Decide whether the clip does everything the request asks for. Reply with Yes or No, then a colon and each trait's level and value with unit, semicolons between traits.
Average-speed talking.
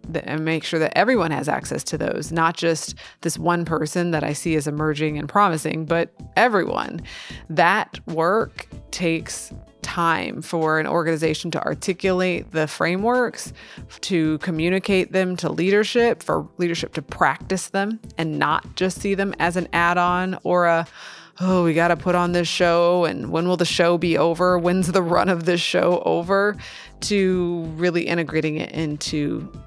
Yes: average, 165 wpm